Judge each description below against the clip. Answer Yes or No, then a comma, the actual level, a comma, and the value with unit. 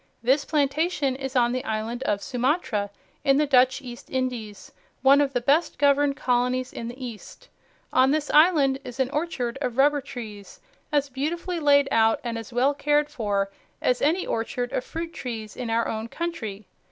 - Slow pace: No, average, 175 wpm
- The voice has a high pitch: Yes, very high, 260 Hz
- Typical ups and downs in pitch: Yes, average, 3.5 semitones